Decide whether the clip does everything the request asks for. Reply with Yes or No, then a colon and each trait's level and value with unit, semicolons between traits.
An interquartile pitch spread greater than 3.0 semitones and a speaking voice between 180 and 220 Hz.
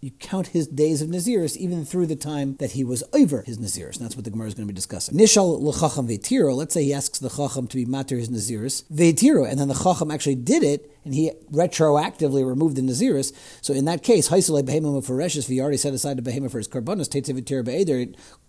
No: average, 3.5 semitones; medium, 140 Hz